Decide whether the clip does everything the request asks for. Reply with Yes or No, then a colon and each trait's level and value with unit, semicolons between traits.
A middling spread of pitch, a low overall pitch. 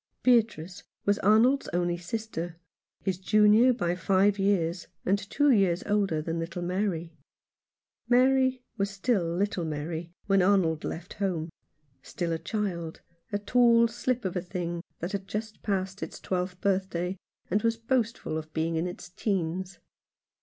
No: average, 3.6 semitones; high, 190 Hz